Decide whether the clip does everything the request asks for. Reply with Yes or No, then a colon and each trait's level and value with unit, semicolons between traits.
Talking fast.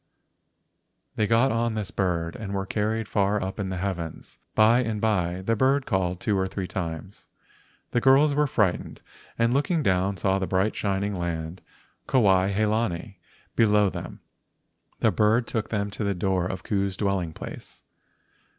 No: average, 165 wpm